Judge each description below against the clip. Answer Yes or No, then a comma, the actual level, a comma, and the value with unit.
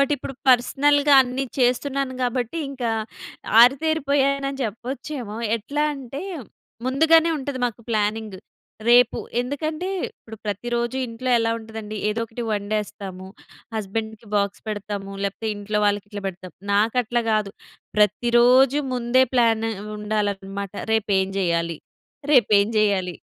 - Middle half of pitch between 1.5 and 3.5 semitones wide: No, average, 4.0 semitones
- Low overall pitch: No, high, 230 Hz